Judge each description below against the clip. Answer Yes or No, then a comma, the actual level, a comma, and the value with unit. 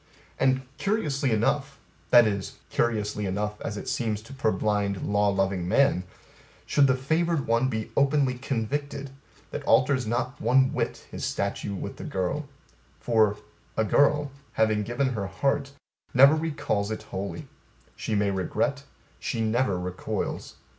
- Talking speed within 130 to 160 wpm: Yes, average, 145 wpm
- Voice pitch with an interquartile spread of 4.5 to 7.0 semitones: Yes, average, 5.0 semitones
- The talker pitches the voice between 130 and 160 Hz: No, low, 120 Hz